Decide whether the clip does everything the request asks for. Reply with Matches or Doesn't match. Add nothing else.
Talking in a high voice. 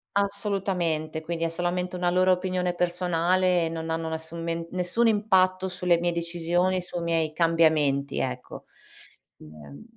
Doesn't match